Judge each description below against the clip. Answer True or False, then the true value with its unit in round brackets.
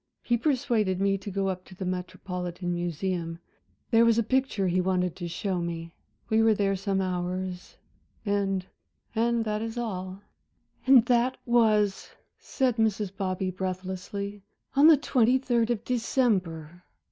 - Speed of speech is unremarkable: True (145 wpm)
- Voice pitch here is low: False (195 Hz)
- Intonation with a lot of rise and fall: False (3.9 semitones)